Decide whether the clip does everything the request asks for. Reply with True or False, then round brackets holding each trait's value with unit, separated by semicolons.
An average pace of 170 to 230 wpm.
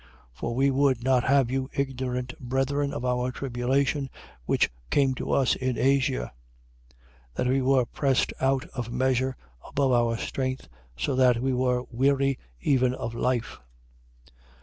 False (150 wpm)